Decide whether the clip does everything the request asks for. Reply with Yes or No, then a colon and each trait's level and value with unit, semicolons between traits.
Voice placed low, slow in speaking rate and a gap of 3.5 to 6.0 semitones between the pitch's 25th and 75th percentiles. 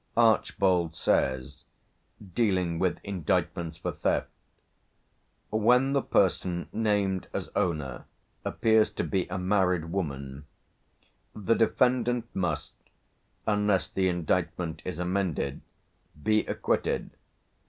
Yes: very low, 95 Hz; slow, 100 wpm; average, 4.0 semitones